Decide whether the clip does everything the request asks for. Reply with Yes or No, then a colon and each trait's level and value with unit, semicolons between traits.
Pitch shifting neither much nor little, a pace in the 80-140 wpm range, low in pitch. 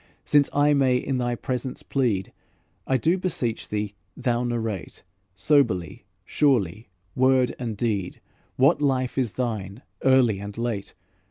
Yes: average, 4.0 semitones; slow, 135 wpm; low, 120 Hz